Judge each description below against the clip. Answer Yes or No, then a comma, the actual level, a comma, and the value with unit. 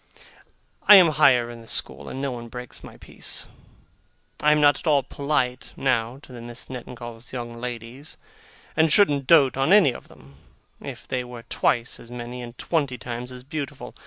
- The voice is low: Yes, low, 125 Hz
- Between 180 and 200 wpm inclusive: Yes, average, 185 wpm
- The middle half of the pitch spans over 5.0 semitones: No, average, 3.0 semitones